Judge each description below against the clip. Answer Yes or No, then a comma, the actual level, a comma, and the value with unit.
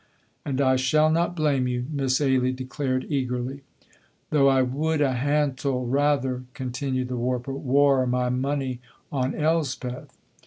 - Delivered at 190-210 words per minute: No, average, 140 wpm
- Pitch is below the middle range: Yes, low, 130 Hz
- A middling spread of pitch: No, narrow, 2.1 semitones